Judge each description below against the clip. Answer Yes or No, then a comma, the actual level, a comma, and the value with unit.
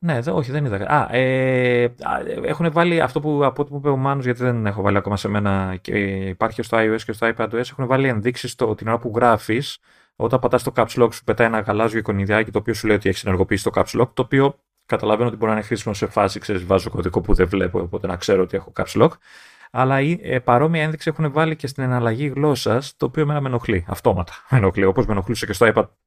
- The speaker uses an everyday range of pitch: Yes, average, 4.2 semitones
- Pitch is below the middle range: Yes, low, 120 Hz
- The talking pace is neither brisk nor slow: No, fast, 245 wpm